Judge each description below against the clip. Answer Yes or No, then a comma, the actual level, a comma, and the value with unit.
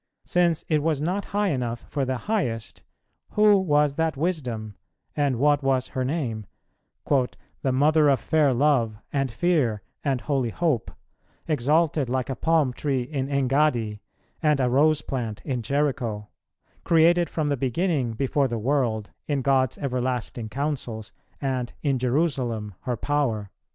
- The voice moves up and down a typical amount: Yes, average, 3.8 semitones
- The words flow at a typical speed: Yes, average, 145 wpm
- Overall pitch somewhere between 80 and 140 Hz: Yes, low, 135 Hz